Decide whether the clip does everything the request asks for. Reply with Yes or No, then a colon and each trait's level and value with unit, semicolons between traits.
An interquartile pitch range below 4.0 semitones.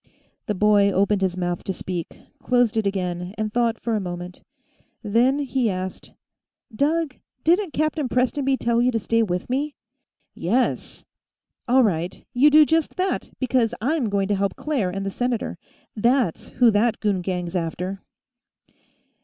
No: average, 5.2 semitones